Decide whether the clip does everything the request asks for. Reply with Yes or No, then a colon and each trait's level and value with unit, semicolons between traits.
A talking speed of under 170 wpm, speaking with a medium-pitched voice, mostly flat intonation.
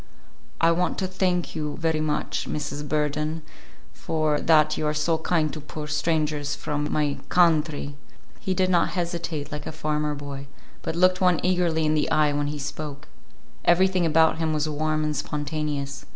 No: average, 175 wpm; medium, 155 Hz; narrow, 1.9 semitones